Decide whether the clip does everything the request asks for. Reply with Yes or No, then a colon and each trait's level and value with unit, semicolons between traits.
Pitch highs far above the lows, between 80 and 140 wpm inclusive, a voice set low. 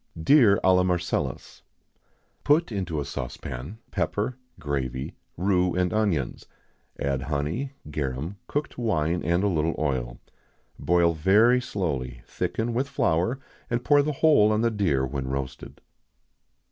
Yes: wide, 7.6 semitones; slow, 135 wpm; very low, 90 Hz